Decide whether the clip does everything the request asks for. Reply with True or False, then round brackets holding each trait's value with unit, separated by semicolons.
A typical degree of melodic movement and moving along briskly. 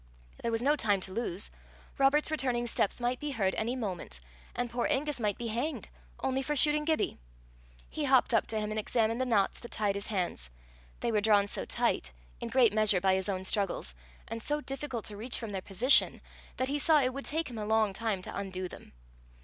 True (4.5 semitones; 215 wpm)